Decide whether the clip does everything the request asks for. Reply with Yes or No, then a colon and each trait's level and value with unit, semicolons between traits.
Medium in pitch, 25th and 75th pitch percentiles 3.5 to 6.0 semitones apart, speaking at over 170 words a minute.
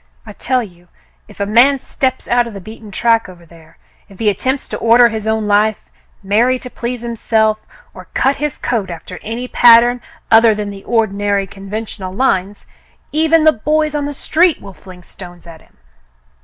No: high, 220 Hz; average, 3.9 semitones; average, 190 wpm